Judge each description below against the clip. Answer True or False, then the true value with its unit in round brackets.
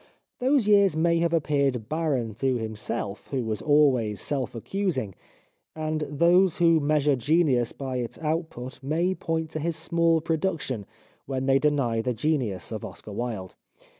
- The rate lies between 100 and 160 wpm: True (150 wpm)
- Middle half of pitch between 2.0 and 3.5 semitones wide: False (5.0 semitones)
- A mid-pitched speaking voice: True (145 Hz)